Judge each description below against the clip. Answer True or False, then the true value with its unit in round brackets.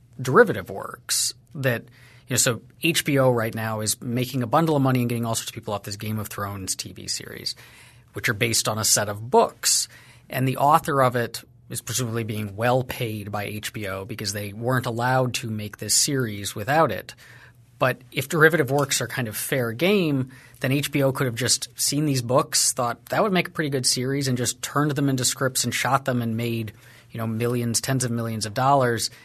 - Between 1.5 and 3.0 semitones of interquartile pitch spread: True (2.6 semitones)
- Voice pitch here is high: False (120 Hz)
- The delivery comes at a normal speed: False (210 wpm)